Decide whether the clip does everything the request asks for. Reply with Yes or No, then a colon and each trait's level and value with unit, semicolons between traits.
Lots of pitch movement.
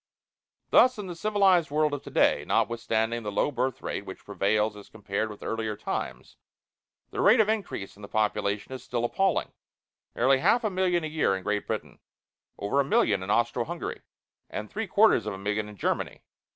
Yes: wide, 8.7 semitones